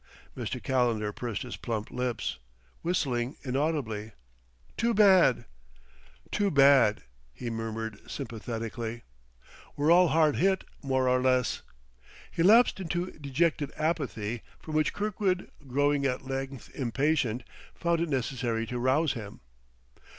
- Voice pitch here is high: No, low, 135 Hz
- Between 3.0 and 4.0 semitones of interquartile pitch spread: No, average, 5.2 semitones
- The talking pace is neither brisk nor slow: No, slow, 120 wpm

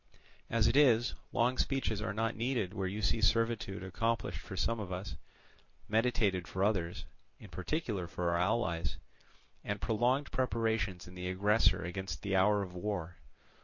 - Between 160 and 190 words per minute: No, average, 150 wpm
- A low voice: Yes, low, 105 Hz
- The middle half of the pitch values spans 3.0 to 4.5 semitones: Yes, average, 3.7 semitones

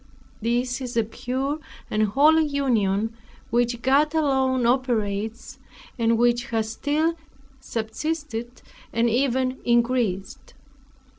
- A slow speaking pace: Yes, slow, 100 wpm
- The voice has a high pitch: Yes, high, 240 Hz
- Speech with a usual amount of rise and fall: Yes, average, 3.0 semitones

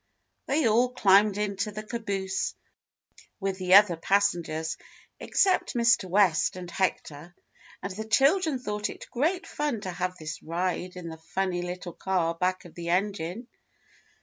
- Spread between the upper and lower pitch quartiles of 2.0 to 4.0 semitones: Yes, average, 3.4 semitones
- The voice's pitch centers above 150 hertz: Yes, high, 190 Hz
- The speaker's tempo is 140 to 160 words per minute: Yes, average, 150 wpm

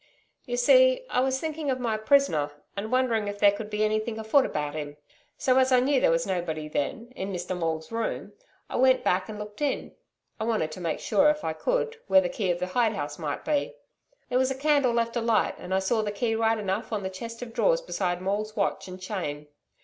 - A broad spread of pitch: Yes, wide, 5.8 semitones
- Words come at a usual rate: No, fast, 230 wpm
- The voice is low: No, high, 220 Hz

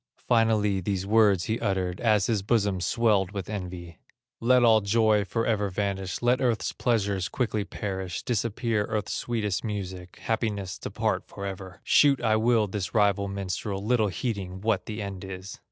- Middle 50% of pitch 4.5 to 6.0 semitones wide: No, average, 2.8 semitones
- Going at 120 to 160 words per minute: Yes, average, 155 wpm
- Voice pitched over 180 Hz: No, low, 105 Hz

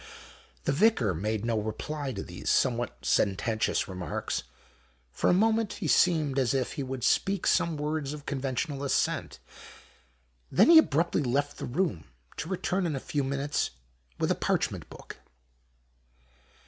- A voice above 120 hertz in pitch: Yes, medium, 140 Hz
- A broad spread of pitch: Yes, wide, 5.8 semitones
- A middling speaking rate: Yes, average, 150 wpm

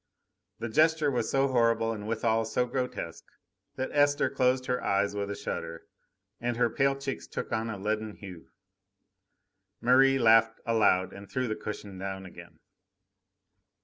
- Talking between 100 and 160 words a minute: Yes, average, 150 wpm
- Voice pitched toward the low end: Yes, low, 115 Hz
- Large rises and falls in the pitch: No, average, 3.9 semitones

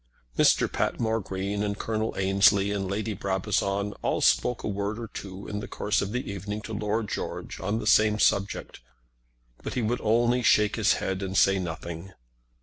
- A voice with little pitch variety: Yes, narrow, 1.9 semitones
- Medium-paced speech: Yes, average, 180 wpm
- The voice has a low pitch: Yes, low, 100 Hz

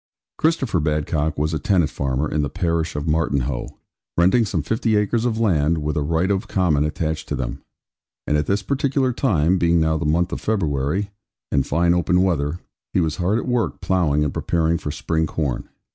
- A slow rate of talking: No, average, 190 wpm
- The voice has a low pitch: Yes, very low, 85 Hz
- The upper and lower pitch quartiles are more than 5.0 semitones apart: No, average, 4.3 semitones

